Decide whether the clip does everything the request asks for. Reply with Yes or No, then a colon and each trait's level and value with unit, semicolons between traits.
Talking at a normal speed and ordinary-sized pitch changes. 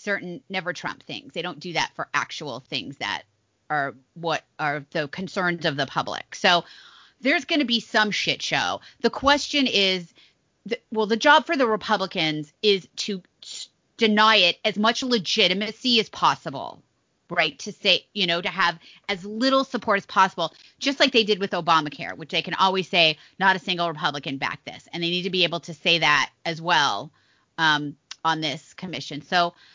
Yes: average, 190 wpm; average, 4.9 semitones